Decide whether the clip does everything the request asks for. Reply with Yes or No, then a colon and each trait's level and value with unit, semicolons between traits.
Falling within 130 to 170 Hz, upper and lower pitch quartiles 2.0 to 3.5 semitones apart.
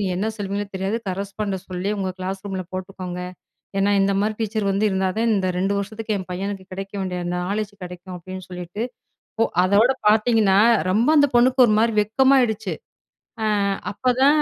No: high, 200 Hz; narrow, 2.6 semitones